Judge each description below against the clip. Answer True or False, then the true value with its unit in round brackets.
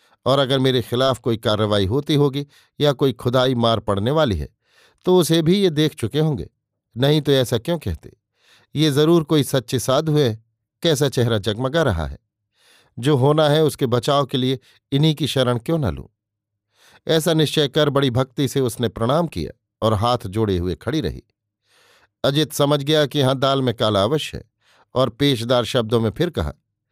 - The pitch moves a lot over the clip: False (4.6 semitones)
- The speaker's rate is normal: True (180 wpm)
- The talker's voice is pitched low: True (130 Hz)